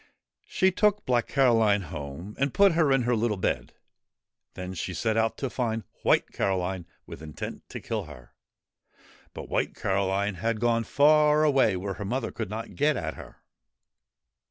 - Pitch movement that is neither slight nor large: No, wide, 5.9 semitones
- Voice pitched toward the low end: Yes, low, 115 Hz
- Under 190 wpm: Yes, average, 165 wpm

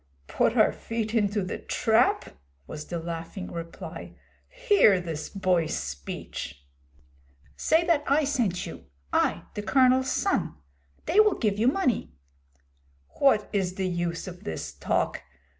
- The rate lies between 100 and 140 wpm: Yes, slow, 135 wpm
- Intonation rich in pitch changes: Yes, wide, 7.7 semitones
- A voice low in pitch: No, high, 200 Hz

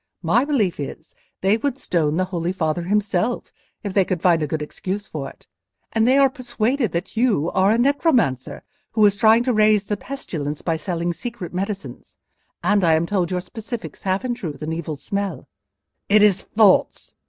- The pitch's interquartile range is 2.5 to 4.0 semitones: No, average, 4.8 semitones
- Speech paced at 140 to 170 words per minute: No, average, 185 wpm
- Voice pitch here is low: No, high, 195 Hz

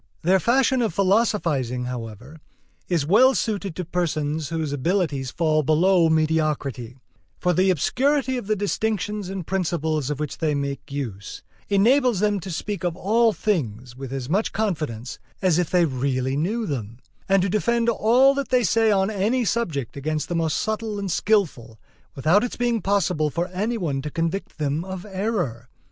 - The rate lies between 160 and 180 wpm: Yes, average, 170 wpm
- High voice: No, medium, 175 Hz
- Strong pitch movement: Yes, wide, 6.3 semitones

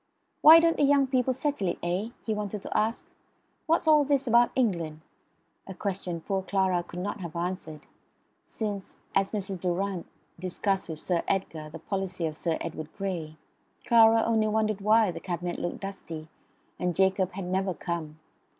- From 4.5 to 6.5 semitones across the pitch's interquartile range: No, average, 3.9 semitones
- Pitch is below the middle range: No, high, 195 Hz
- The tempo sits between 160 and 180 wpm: Yes, average, 170 wpm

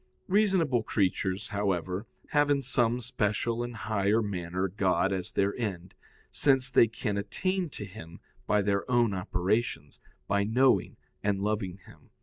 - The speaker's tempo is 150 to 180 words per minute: No, average, 140 wpm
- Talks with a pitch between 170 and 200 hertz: No, low, 105 Hz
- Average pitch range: Yes, average, 3.8 semitones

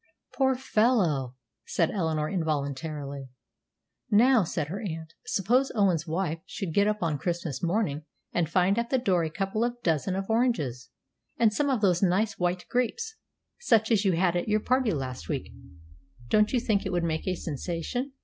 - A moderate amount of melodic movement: No, wide, 5.7 semitones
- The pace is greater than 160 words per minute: Yes, average, 175 wpm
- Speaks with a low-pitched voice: No, medium, 185 Hz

